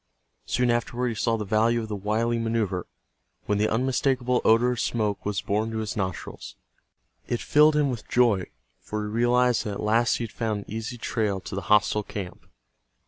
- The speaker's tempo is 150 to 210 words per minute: Yes, average, 195 wpm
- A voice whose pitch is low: Yes, low, 110 Hz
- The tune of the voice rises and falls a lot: No, narrow, 2.5 semitones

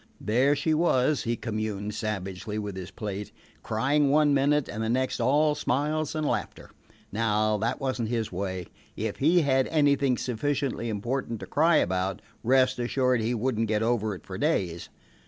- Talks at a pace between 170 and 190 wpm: Yes, average, 175 wpm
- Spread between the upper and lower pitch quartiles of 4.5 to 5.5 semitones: Yes, average, 4.8 semitones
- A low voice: Yes, low, 120 Hz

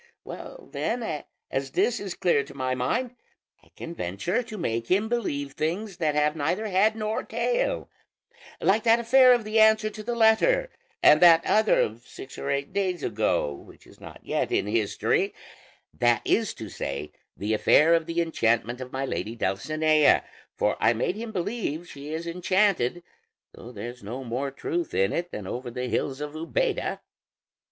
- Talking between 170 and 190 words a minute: Yes, average, 175 wpm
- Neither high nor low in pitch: Yes, medium, 165 Hz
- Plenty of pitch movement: Yes, wide, 8.9 semitones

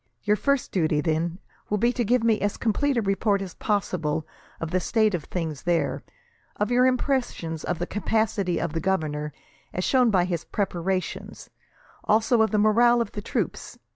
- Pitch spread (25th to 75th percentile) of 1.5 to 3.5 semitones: No, average, 4.7 semitones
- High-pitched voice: Yes, high, 200 Hz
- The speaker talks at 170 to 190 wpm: Yes, average, 180 wpm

